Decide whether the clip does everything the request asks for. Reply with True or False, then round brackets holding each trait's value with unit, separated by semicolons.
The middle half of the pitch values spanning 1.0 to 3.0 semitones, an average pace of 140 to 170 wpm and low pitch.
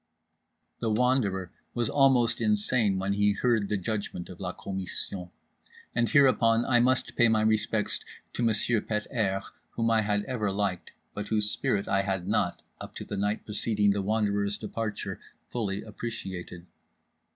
True (2.6 semitones; 160 wpm; 105 Hz)